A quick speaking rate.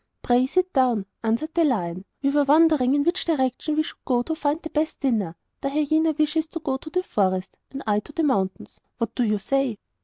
Yes: fast, 220 wpm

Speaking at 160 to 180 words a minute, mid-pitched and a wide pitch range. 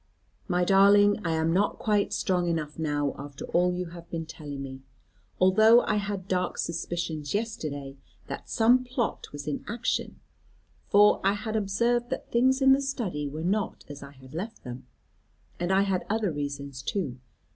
Yes: average, 170 wpm; medium, 180 Hz; wide, 6.2 semitones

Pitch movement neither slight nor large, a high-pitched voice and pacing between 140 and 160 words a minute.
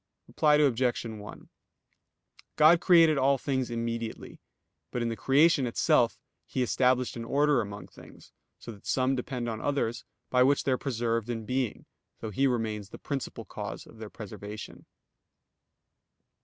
No: average, 3.2 semitones; low, 125 Hz; average, 150 wpm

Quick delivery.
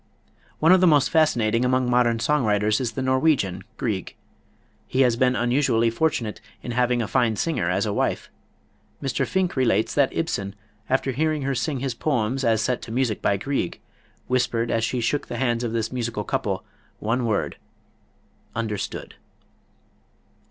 No: average, 165 wpm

